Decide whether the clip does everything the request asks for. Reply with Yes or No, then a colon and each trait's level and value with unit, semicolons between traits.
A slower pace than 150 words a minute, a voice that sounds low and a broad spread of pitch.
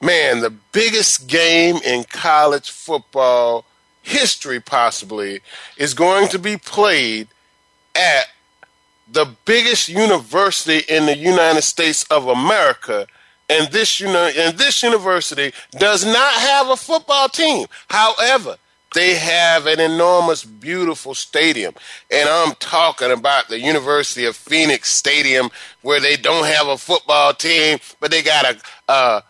No: slow, 135 wpm; medium, 165 Hz; wide, 5.8 semitones